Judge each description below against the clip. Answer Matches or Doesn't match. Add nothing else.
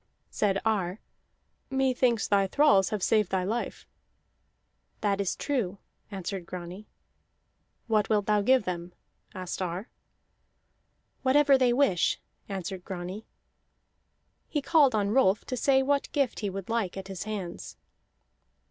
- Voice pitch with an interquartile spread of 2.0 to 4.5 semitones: Doesn't match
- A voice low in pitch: Doesn't match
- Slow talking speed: Matches